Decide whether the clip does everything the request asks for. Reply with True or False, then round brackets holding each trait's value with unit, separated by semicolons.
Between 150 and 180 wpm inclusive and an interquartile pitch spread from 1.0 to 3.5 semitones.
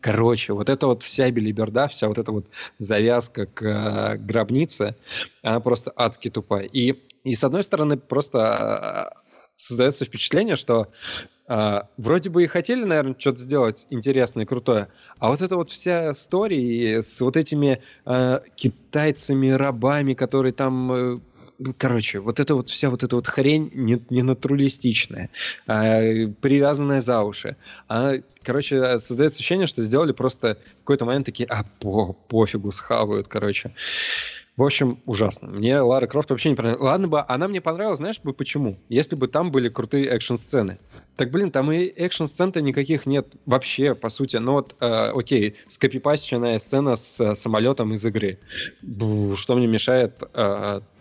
False (160 wpm; 3.9 semitones)